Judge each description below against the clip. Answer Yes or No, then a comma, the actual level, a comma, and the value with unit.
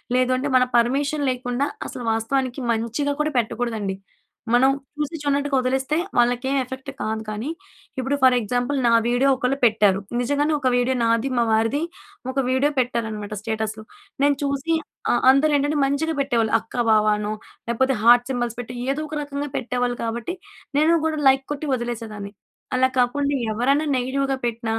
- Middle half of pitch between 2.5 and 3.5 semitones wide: Yes, average, 3.2 semitones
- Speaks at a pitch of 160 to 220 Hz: No, very high, 250 Hz